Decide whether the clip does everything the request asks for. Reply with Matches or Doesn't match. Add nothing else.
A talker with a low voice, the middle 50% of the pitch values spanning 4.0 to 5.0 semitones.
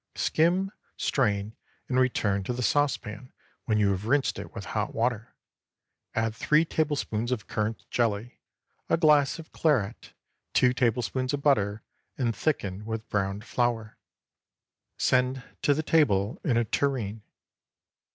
Matches